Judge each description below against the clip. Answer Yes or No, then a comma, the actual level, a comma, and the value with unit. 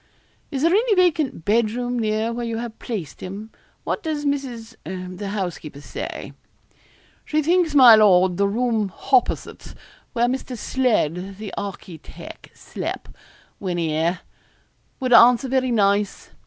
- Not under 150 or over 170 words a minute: No, slow, 135 wpm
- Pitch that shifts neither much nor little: Yes, average, 5.0 semitones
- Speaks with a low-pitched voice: No, high, 225 Hz